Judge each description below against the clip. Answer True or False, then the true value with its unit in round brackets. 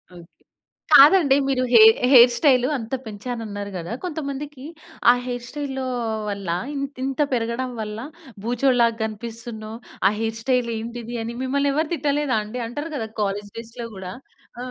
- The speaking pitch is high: True (240 Hz)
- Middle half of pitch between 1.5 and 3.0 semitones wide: False (3.6 semitones)